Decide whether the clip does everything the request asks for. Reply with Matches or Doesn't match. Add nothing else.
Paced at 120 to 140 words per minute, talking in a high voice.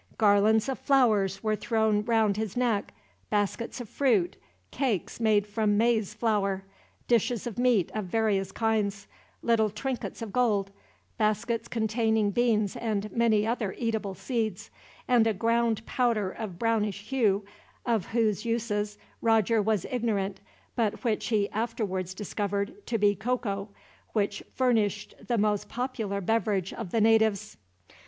Matches